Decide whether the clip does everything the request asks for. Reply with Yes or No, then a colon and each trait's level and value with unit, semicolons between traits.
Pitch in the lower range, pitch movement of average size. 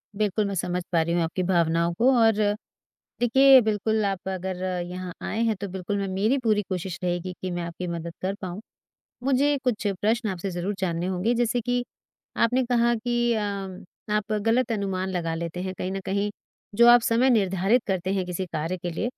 No: high, 195 Hz; average, 4.1 semitones